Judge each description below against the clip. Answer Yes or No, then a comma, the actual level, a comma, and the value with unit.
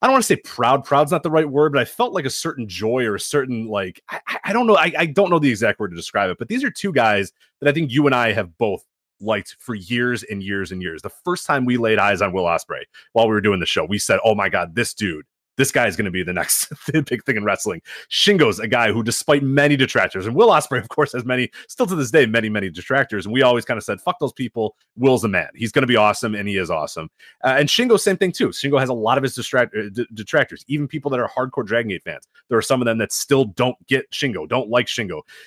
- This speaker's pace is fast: Yes, fast, 290 wpm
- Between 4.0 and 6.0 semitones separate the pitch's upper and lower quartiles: Yes, average, 5.1 semitones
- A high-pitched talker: No, low, 125 Hz